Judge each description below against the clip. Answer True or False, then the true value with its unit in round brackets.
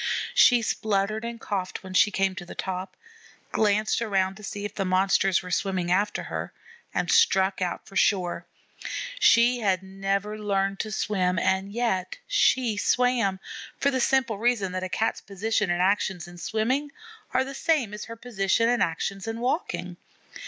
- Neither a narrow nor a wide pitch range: True (3.3 semitones)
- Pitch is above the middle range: True (200 Hz)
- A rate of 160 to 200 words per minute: True (170 wpm)